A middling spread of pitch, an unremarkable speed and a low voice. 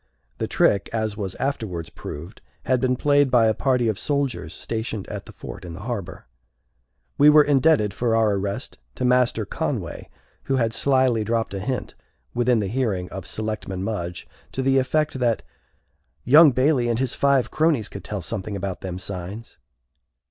Yes: average, 4.8 semitones; average, 170 wpm; low, 115 Hz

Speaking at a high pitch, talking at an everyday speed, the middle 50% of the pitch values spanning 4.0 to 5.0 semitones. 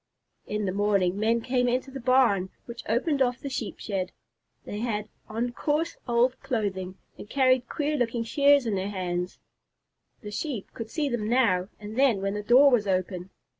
Yes: high, 230 Hz; average, 180 wpm; average, 4.3 semitones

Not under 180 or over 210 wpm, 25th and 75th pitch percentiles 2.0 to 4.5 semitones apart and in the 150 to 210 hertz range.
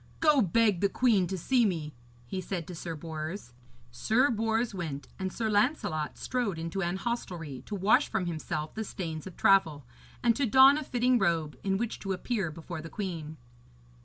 No: average, 185 wpm; wide, 5.6 semitones; high, 190 Hz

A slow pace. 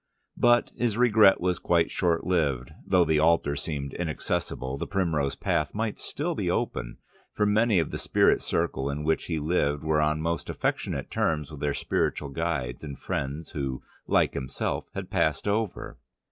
No: average, 170 wpm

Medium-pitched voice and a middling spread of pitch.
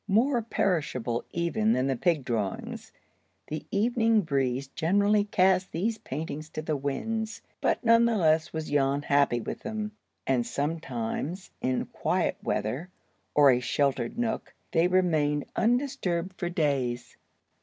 No: medium, 160 Hz; wide, 6.9 semitones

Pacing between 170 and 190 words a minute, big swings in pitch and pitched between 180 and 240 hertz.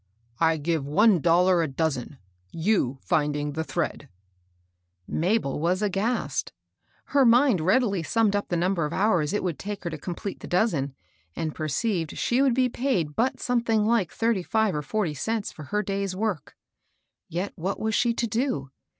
Yes: average, 175 wpm; wide, 5.9 semitones; medium, 185 Hz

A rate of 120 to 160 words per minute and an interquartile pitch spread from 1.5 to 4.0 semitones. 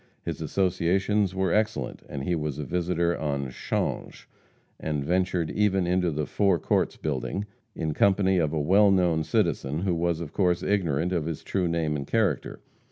No: average, 170 wpm; average, 3.6 semitones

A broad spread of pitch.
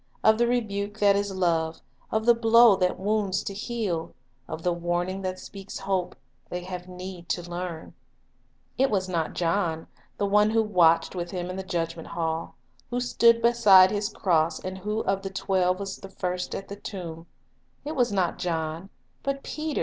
No: average, 3.1 semitones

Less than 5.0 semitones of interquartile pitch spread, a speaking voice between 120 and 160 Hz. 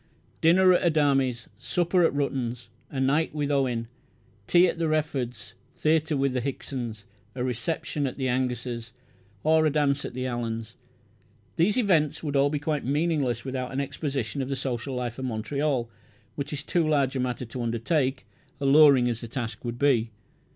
Yes: average, 3.6 semitones; low, 135 Hz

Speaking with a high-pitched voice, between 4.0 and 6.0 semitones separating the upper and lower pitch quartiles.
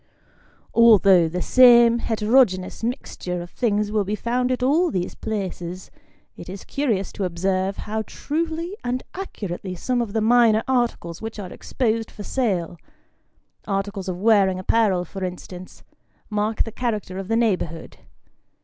Yes: high, 210 Hz; average, 4.3 semitones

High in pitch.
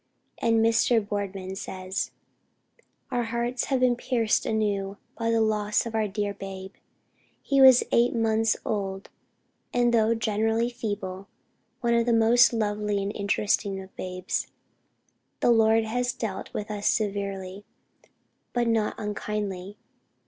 Yes: high, 215 Hz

